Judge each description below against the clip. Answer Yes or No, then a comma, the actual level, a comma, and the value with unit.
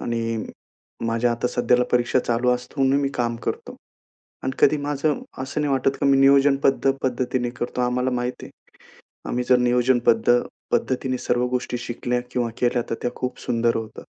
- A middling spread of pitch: No, narrow, 1.5 semitones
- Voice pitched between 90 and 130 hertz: Yes, low, 125 Hz